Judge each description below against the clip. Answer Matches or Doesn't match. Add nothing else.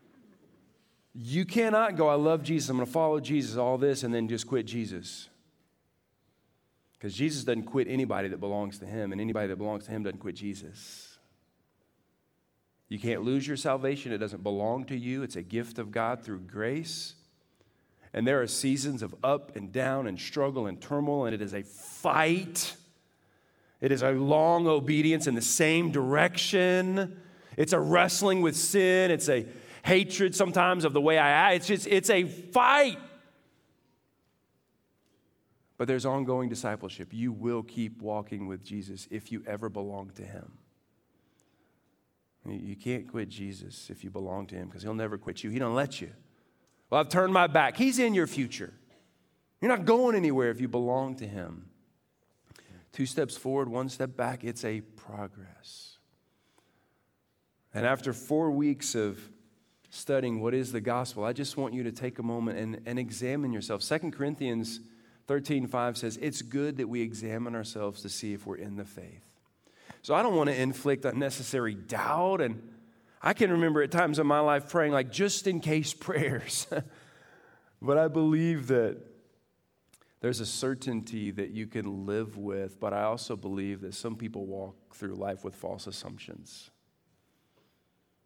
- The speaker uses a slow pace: Doesn't match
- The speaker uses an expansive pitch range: Matches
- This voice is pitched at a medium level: Doesn't match